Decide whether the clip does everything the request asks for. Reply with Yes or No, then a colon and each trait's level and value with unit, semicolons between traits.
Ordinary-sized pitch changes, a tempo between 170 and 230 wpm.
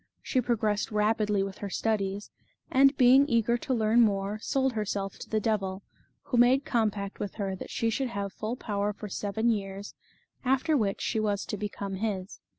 Yes: average, 3.0 semitones; average, 180 wpm